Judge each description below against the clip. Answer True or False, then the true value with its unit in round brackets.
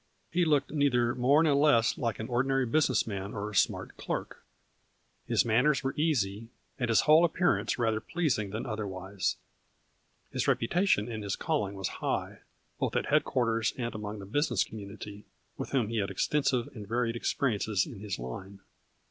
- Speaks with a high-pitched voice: False (115 Hz)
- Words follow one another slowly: False (175 wpm)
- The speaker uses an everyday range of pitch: True (4.7 semitones)